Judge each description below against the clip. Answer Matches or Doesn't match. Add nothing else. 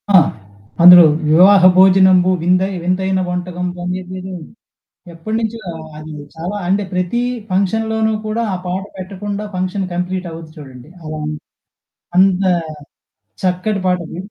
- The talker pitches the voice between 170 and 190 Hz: Matches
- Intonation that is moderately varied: Doesn't match